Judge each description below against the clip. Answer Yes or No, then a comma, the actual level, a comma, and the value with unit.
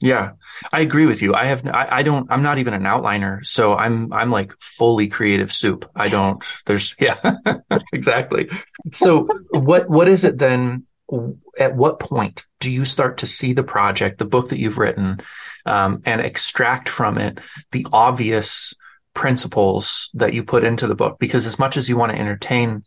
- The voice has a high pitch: No, low, 125 Hz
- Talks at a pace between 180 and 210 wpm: Yes, average, 185 wpm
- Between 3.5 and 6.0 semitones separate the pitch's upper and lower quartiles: Yes, average, 4.6 semitones